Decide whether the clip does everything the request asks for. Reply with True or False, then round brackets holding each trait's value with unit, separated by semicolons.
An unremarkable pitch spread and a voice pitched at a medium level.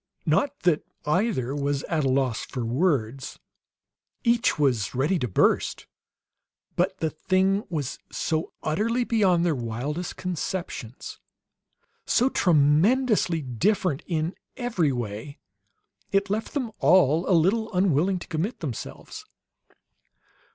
False (5.8 semitones; 165 Hz)